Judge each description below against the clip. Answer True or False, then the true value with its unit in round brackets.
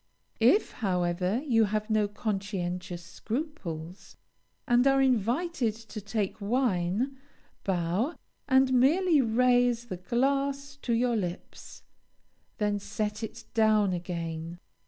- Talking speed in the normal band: False (110 wpm)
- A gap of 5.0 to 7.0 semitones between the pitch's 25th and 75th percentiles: True (5.3 semitones)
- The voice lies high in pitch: True (220 Hz)